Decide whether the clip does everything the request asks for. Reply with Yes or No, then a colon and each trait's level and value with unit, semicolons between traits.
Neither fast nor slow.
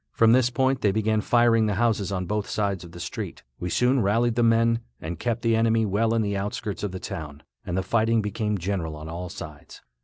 No: fast, 225 wpm